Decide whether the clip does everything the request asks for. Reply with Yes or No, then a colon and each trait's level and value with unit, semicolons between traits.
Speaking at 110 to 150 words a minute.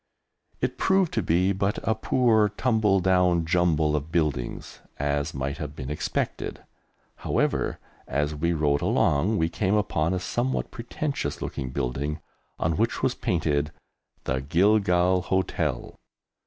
Yes: slow, 135 wpm